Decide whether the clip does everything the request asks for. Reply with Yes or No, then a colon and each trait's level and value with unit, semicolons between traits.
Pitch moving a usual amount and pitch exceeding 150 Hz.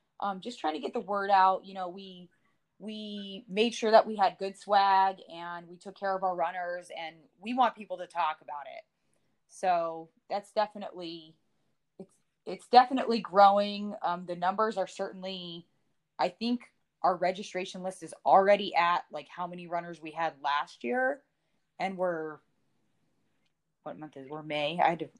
Yes: average, 3.0 semitones; medium, 185 Hz